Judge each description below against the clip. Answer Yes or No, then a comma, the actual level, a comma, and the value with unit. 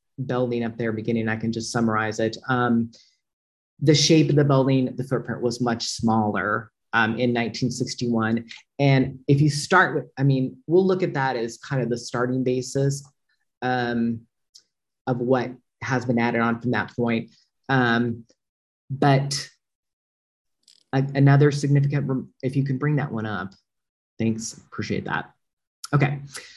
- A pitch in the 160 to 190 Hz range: No, low, 125 Hz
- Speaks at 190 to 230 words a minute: No, average, 150 wpm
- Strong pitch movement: No, average, 3.0 semitones